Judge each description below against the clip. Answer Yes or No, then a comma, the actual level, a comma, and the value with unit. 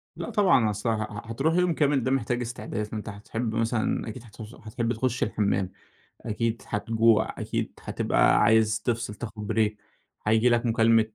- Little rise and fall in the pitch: Yes, narrow, 2.0 semitones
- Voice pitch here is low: Yes, low, 115 Hz